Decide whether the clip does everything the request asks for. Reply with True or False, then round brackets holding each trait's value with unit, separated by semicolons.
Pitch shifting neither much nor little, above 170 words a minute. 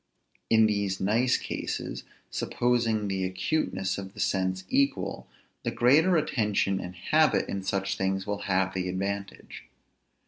False (3.3 semitones; 135 wpm)